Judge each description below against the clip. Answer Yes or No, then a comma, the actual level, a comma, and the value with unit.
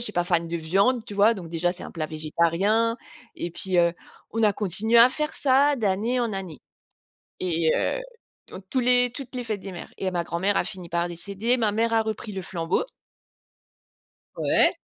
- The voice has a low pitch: No, high, 200 Hz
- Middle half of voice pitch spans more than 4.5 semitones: Yes, average, 4.9 semitones